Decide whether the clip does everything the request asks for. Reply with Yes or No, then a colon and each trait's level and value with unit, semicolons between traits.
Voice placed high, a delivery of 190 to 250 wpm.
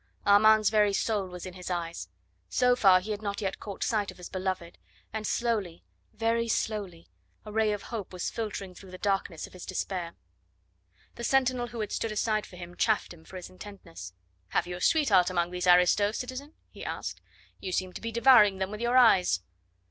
Yes: high, 200 Hz; average, 200 wpm